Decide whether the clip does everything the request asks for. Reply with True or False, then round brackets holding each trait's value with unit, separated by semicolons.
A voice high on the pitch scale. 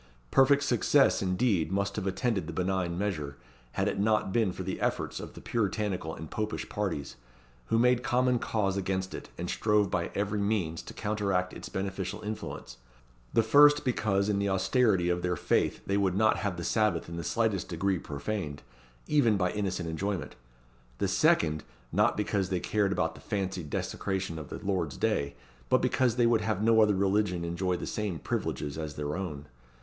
False (95 Hz)